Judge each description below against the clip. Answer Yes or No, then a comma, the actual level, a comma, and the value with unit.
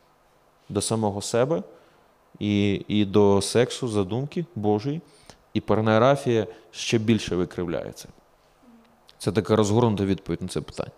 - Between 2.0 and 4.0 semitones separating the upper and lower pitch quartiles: Yes, average, 2.7 semitones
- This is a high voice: No, low, 110 Hz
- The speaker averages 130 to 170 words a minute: No, average, 115 wpm